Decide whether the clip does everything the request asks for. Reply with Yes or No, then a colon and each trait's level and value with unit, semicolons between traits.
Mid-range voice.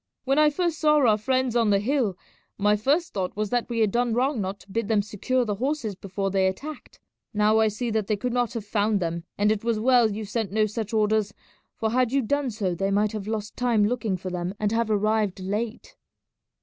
No: high, 215 Hz